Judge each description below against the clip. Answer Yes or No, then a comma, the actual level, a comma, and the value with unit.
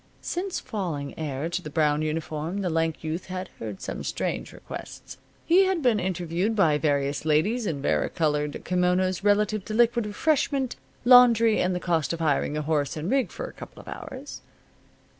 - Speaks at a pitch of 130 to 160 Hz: No, medium, 180 Hz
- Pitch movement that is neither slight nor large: No, wide, 6.4 semitones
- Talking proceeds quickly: No, average, 175 wpm